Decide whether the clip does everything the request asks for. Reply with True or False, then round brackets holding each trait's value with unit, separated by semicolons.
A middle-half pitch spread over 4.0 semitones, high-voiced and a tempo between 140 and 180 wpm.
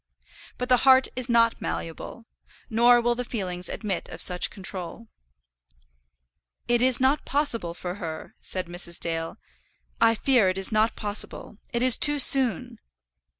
True (5.3 semitones; 230 Hz; 150 wpm)